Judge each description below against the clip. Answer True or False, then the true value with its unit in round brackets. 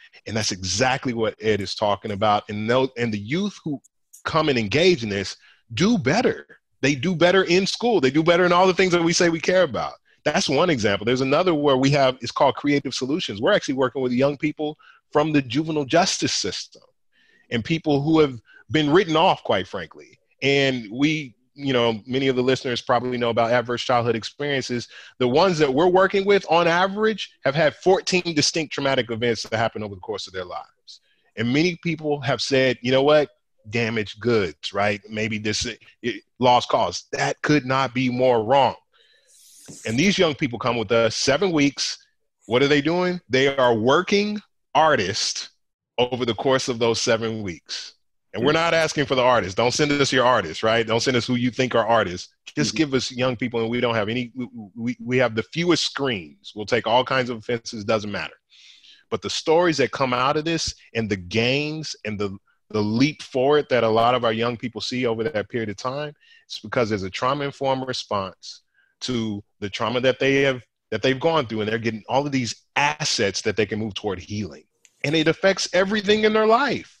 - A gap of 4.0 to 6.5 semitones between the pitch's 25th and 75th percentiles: True (5.1 semitones)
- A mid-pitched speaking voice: False (130 Hz)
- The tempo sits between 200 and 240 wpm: True (205 wpm)